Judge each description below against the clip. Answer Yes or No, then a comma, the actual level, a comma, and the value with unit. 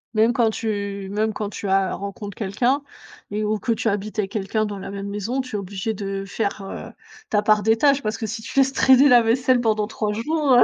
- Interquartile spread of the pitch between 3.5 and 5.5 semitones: No, average, 2.8 semitones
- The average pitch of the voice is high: Yes, high, 215 Hz